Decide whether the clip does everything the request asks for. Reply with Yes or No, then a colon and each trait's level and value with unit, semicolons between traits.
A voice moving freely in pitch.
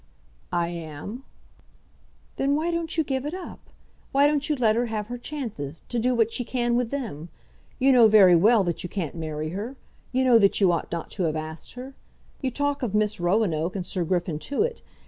Yes: wide, 7.2 semitones